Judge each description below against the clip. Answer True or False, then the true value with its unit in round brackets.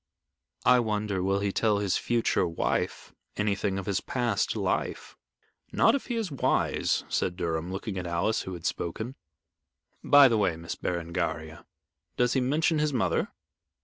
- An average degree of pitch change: False (5.7 semitones)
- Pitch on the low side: True (100 Hz)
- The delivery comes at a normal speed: True (155 wpm)